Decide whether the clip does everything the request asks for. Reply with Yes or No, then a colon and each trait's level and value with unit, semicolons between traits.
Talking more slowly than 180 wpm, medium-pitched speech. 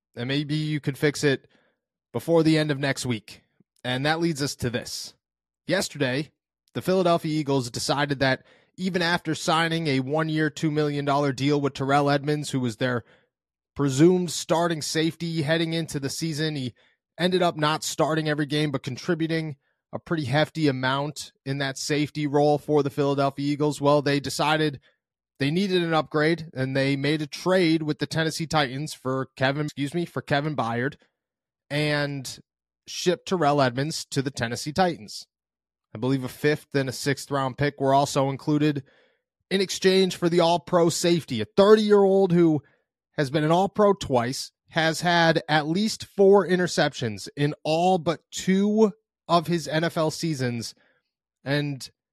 Yes: average, 165 wpm; medium, 150 Hz